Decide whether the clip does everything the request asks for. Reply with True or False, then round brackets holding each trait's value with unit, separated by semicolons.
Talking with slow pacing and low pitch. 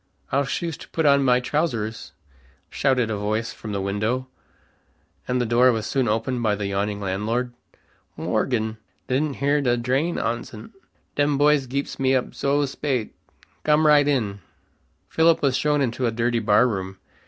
False (160 wpm; 125 Hz)